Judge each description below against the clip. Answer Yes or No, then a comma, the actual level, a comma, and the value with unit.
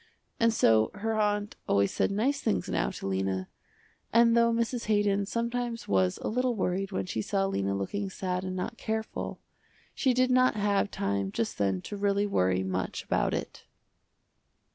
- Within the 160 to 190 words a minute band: Yes, average, 170 wpm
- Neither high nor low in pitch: No, high, 200 Hz